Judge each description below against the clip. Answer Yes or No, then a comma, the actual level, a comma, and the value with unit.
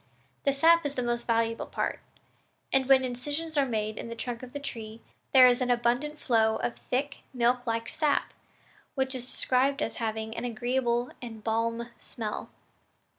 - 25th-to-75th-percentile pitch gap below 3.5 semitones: Yes, average, 2.7 semitones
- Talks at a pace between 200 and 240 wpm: No, average, 175 wpm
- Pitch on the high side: Yes, high, 245 Hz